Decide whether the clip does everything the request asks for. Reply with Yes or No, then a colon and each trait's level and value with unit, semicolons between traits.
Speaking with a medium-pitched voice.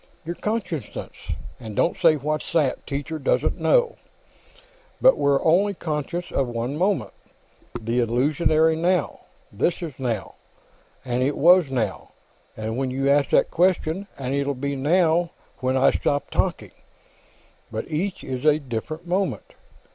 Yes: medium, 150 Hz